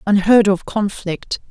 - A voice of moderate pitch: No, high, 200 Hz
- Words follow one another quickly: No, slow, 120 wpm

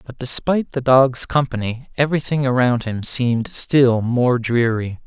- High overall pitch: No, low, 125 Hz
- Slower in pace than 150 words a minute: Yes, average, 140 wpm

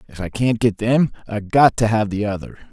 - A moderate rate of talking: No, fast, 245 wpm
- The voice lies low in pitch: Yes, low, 110 Hz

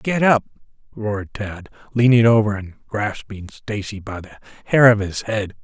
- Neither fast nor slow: Yes, average, 160 wpm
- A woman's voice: No, male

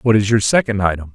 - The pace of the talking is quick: Yes, fast, 260 wpm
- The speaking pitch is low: Yes, low, 105 Hz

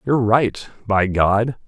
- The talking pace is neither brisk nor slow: Yes, average, 145 wpm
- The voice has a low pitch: Yes, low, 110 Hz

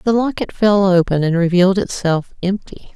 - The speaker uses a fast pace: No, average, 140 wpm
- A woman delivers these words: Yes, female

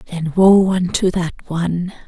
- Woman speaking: Yes, female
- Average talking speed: Yes, average, 145 wpm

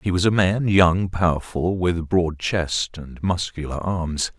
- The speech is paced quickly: No, average, 165 wpm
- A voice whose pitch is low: Yes, very low, 90 Hz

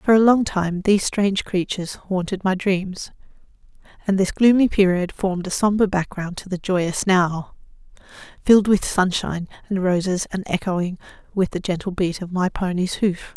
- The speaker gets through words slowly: No, average, 165 wpm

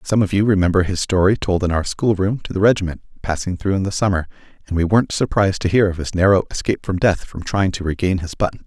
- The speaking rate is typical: No, fast, 250 wpm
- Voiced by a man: Yes, male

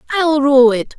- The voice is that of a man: No, female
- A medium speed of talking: Yes, average, 180 wpm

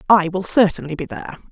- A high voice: No, medium, 175 Hz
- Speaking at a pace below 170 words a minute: No, average, 200 wpm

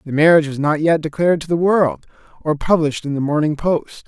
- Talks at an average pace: No, fast, 220 wpm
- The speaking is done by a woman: No, male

